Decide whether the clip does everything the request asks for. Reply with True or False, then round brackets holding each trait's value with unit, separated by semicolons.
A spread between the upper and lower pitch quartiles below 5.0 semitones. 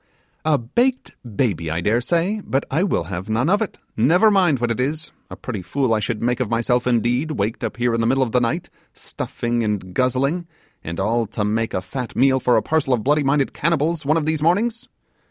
False (5.5 semitones)